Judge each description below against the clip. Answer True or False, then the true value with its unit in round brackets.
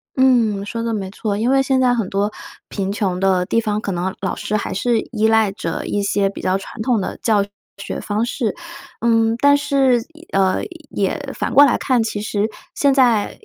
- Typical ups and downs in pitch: True (3.6 semitones)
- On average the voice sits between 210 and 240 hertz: True (220 Hz)